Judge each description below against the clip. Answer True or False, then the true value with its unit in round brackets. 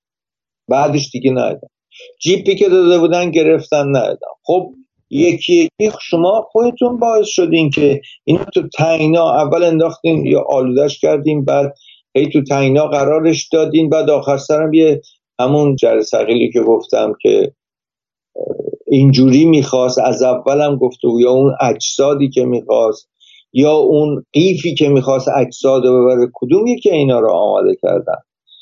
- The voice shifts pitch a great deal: True (7.5 semitones)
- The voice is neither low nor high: True (155 Hz)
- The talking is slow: False (135 wpm)